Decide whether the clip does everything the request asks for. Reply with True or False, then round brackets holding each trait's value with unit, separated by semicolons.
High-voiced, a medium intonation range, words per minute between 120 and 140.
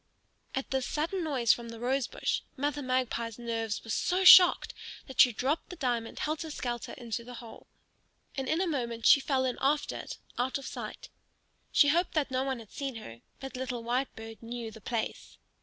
False (255 Hz; 3.4 semitones; 190 wpm)